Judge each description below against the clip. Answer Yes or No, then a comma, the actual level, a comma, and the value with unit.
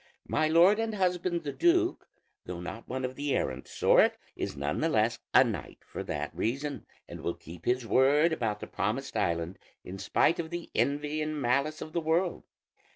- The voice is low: No, medium, 145 Hz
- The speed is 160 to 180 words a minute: No, average, 190 wpm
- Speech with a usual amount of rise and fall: No, wide, 6.9 semitones